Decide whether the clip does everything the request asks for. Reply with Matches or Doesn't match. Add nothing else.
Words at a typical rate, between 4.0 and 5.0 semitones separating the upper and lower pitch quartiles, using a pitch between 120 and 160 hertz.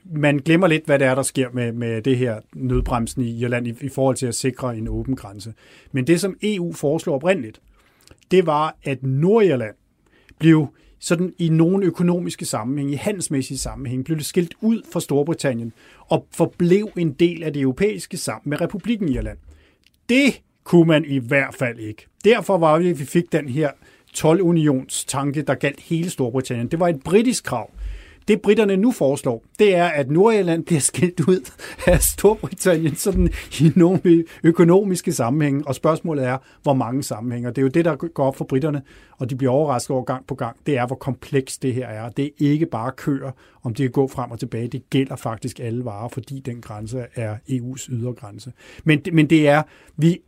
Matches